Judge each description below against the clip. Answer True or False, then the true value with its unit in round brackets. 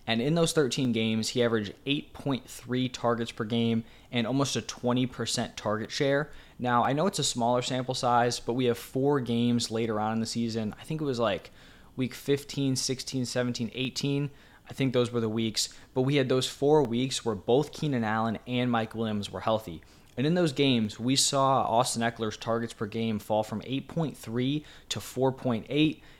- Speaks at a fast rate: False (190 wpm)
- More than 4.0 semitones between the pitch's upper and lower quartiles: False (2.9 semitones)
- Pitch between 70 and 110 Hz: False (120 Hz)